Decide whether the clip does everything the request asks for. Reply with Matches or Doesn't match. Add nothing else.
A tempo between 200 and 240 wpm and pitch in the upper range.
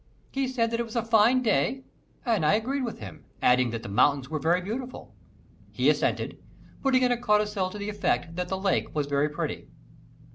Matches